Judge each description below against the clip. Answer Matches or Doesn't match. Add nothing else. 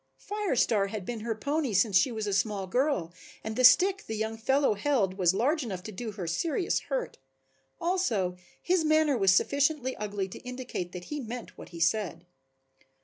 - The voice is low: Doesn't match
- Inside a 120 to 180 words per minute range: Doesn't match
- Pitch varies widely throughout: Matches